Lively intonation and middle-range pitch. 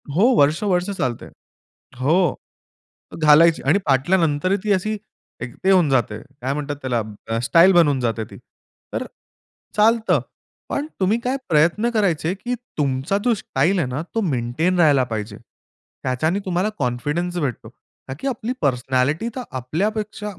Yes: wide, 6.8 semitones; medium, 160 Hz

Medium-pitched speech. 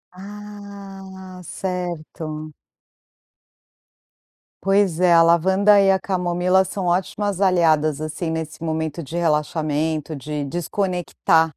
Yes: medium, 175 Hz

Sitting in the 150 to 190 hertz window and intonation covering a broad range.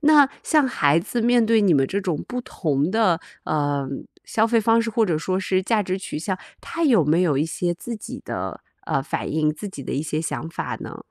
Yes: medium, 185 Hz; wide, 6.6 semitones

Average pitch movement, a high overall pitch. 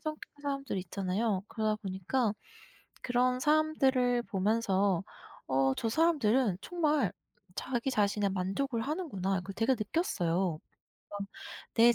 No: wide, 5.7 semitones; high, 225 Hz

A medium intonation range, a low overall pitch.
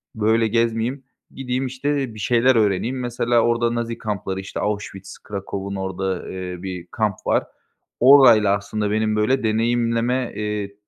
Yes: average, 3.2 semitones; low, 110 Hz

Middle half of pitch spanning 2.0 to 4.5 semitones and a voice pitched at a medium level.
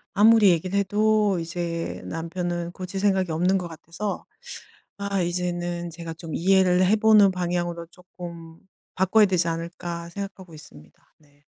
Yes: narrow, 2.4 semitones; medium, 175 Hz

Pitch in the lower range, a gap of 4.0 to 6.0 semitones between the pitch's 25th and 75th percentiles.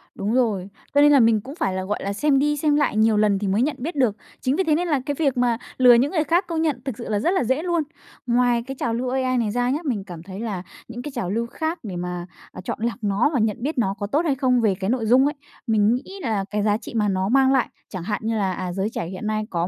No: high, 235 Hz; average, 4.9 semitones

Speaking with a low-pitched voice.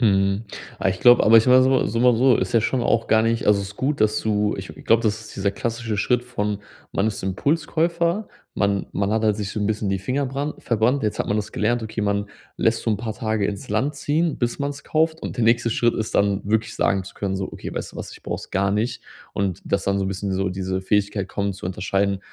Yes: low, 110 Hz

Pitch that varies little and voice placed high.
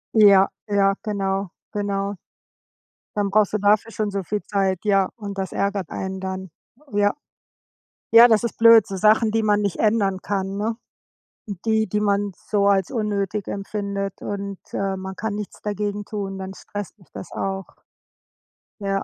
Yes: narrow, 1.4 semitones; high, 200 Hz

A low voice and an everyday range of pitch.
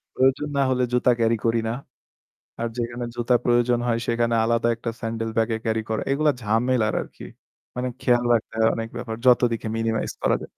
No: low, 115 Hz; narrow, 1.4 semitones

